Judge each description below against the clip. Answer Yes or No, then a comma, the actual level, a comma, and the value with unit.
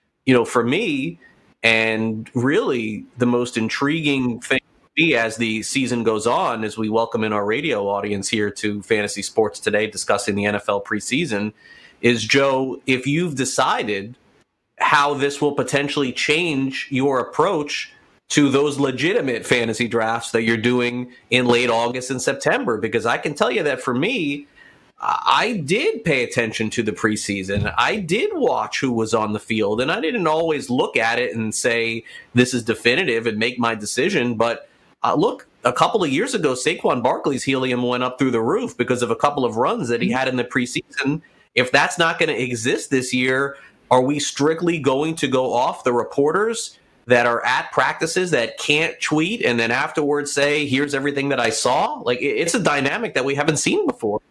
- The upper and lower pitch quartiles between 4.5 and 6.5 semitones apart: No, average, 3.7 semitones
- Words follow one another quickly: No, average, 185 wpm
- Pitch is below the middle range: Yes, low, 125 Hz